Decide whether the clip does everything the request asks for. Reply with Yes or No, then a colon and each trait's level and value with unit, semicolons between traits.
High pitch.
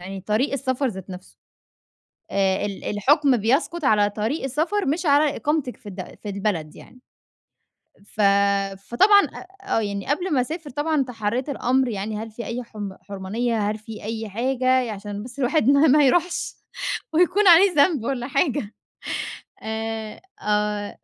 Yes: high, 240 Hz